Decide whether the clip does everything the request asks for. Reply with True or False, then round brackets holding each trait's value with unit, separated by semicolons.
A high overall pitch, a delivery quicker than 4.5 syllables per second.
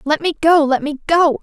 True (300 Hz; 5.1 syllables/s)